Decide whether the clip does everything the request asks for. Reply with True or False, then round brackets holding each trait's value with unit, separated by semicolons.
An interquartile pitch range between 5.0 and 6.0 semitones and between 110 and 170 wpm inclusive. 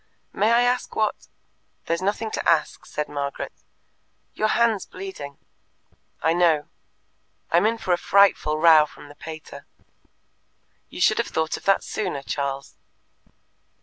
True (5.3 semitones; 145 wpm)